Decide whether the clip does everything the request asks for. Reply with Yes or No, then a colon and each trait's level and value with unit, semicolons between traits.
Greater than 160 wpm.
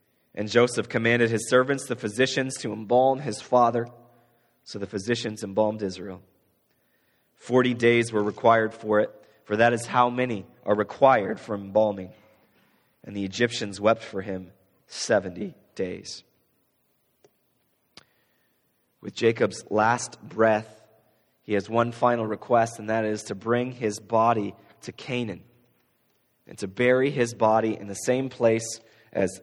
No: slow, 135 wpm